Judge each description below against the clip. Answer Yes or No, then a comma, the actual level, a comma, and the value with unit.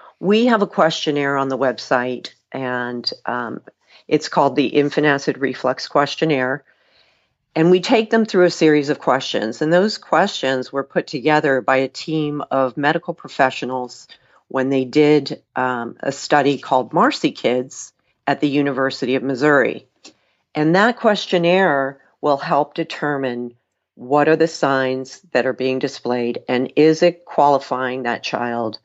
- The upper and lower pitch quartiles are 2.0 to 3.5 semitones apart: Yes, average, 3.0 semitones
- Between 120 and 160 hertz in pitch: Yes, medium, 140 Hz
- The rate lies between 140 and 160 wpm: Yes, average, 150 wpm